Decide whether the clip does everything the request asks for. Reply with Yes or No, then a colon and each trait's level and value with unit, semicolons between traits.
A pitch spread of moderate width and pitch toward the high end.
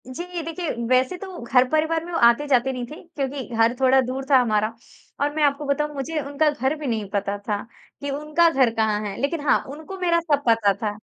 Yes: average, 4.6 semitones; very high, 275 Hz